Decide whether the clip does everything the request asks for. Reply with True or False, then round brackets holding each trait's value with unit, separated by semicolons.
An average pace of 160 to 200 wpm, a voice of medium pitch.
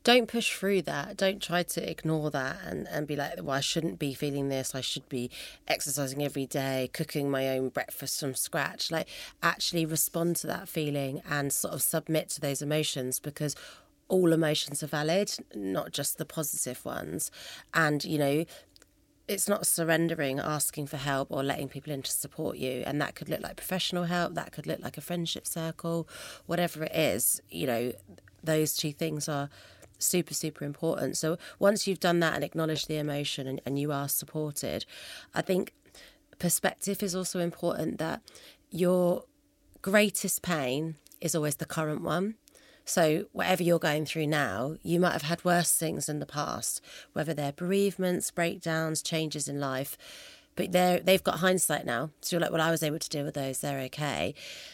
True (180 wpm; 160 Hz)